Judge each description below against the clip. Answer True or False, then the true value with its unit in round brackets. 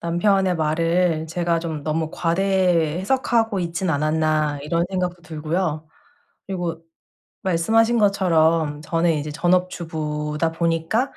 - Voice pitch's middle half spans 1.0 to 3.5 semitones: True (2.6 semitones)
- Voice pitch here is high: False (165 Hz)